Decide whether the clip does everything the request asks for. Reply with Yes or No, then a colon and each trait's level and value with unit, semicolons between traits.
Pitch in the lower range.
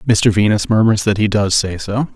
Yes: low, 105 Hz